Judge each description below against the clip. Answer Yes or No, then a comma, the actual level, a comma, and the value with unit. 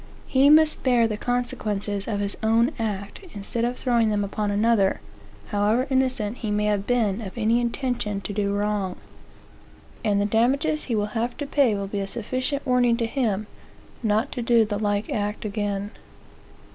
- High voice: Yes, high, 220 Hz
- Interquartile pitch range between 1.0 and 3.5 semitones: Yes, average, 3.0 semitones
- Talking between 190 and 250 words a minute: No, average, 175 wpm